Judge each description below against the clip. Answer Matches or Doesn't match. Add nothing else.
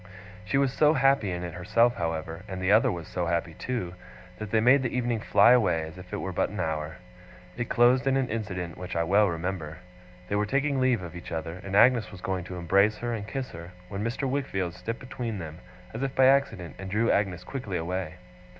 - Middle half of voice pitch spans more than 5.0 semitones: Matches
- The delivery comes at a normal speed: Doesn't match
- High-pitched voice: Doesn't match